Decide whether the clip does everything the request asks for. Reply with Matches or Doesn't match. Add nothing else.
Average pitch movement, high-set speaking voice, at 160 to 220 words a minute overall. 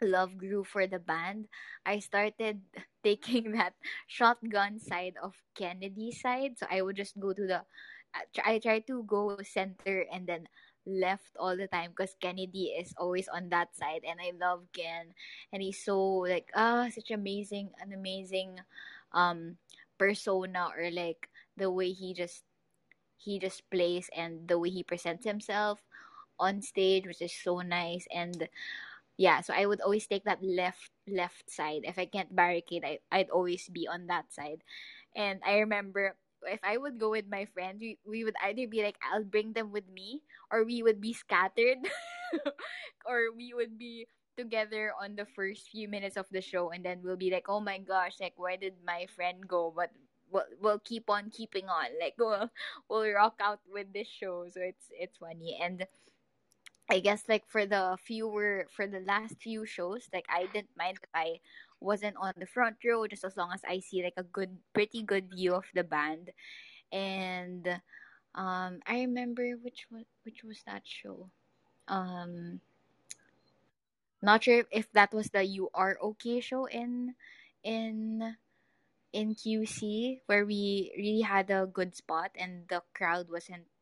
Matches